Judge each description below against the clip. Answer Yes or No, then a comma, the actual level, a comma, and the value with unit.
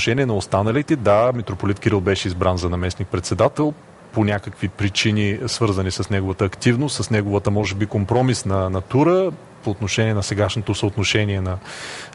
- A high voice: No, low, 105 Hz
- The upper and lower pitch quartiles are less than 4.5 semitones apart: Yes, average, 2.8 semitones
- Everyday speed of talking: Yes, average, 145 wpm